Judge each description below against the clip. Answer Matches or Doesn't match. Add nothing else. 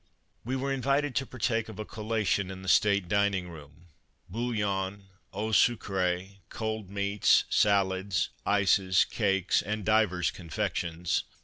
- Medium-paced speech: Doesn't match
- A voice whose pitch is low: Matches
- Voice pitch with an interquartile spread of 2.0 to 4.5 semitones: Matches